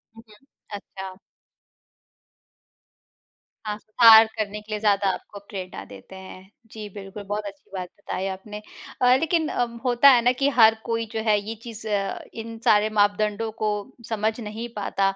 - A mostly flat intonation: Yes, narrow, 2.1 semitones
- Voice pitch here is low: No, high, 215 Hz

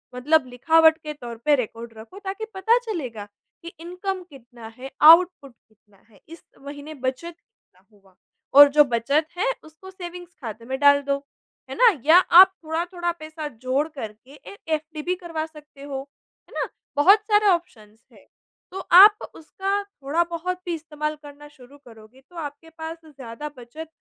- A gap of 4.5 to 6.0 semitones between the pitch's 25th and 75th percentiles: Yes, average, 4.8 semitones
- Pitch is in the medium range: No, very high, 305 Hz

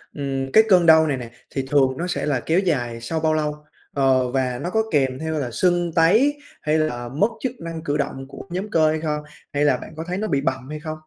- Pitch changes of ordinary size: Yes, average, 3.8 semitones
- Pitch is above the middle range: No, medium, 150 Hz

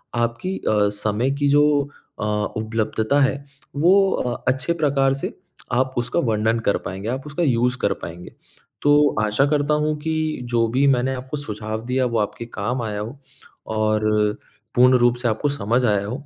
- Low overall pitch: Yes, low, 120 Hz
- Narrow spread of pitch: No, average, 3.9 semitones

